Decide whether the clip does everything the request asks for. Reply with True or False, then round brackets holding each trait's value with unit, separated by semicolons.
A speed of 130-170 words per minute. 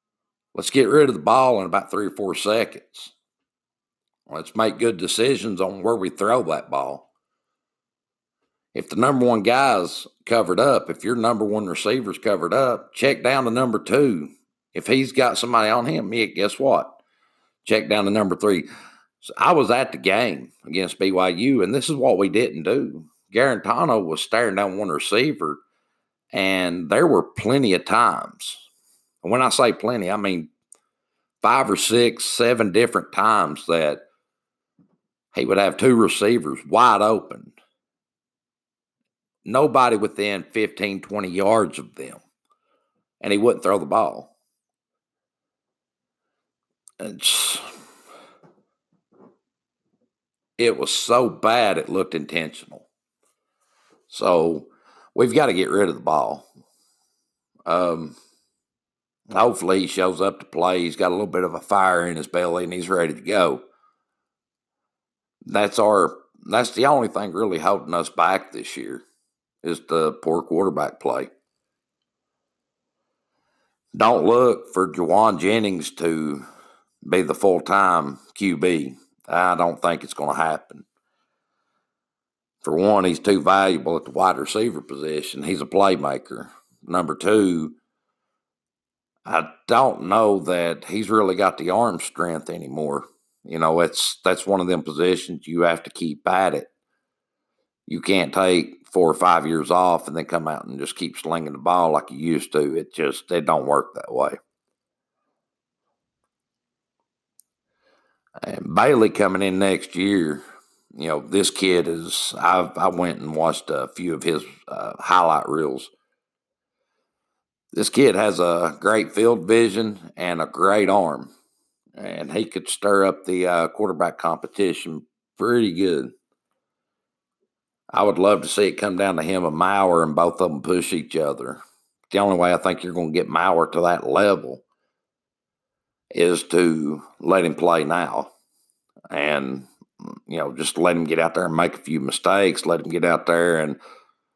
True (150 wpm)